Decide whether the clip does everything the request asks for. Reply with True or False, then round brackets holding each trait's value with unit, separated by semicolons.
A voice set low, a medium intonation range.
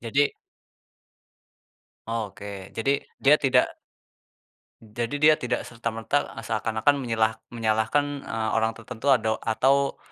True (115 Hz; 3.8 semitones)